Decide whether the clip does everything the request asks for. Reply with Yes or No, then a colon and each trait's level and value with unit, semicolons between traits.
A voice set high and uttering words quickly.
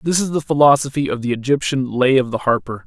No: low, 135 Hz; fast, 230 wpm